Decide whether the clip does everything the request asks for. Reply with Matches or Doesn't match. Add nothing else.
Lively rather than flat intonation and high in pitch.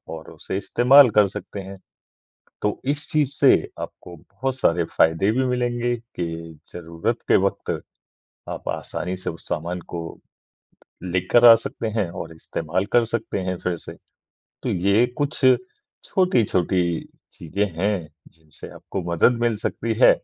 Doesn't match